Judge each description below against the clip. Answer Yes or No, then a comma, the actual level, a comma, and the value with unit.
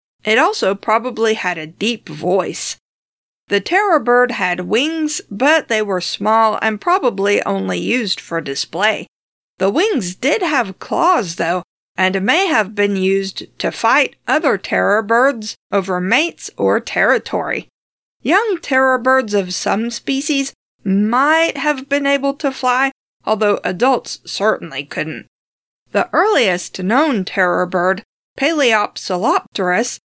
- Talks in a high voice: Yes, high, 220 Hz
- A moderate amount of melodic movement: No, wide, 6.1 semitones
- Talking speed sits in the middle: No, slow, 130 wpm